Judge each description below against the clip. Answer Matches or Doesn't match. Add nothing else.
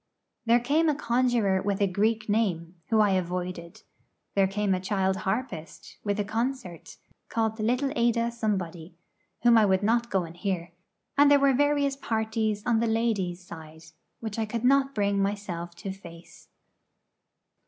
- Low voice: Doesn't match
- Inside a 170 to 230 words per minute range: Doesn't match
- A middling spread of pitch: Matches